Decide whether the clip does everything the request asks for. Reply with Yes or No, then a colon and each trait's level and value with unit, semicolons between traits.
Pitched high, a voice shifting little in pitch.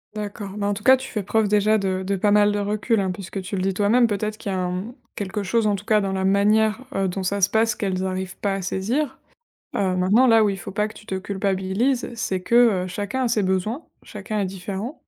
Yes: high, 205 Hz; narrow, 2.3 semitones